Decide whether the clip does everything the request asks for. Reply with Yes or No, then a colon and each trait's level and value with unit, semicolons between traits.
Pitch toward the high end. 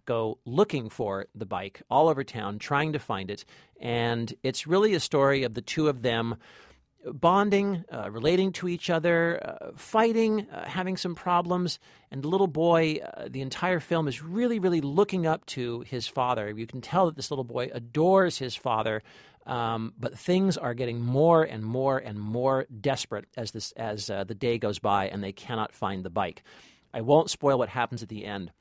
No: low, 135 Hz